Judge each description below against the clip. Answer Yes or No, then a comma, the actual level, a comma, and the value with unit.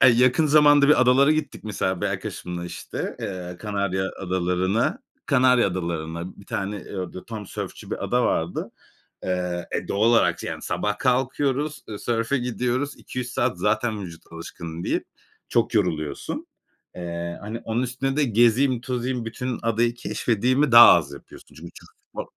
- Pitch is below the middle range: Yes, low, 115 Hz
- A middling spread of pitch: No, wide, 5.7 semitones